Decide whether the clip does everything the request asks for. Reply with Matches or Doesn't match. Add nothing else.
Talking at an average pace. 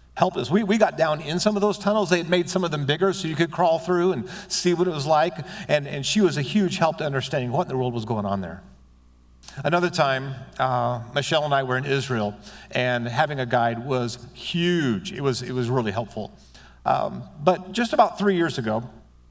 Doesn't match